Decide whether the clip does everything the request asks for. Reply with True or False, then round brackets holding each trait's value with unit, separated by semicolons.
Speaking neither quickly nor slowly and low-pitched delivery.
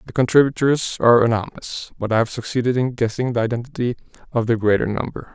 True (180 wpm; 120 Hz)